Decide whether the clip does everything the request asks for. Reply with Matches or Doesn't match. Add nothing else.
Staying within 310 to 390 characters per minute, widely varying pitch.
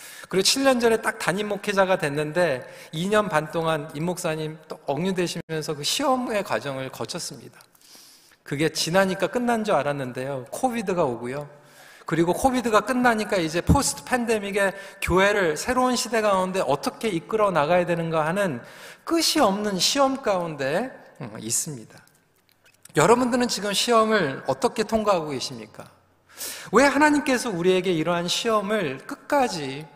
Matches